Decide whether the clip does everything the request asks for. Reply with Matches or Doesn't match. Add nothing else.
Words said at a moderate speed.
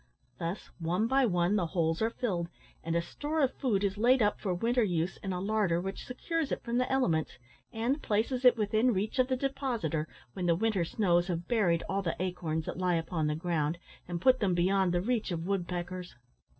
Doesn't match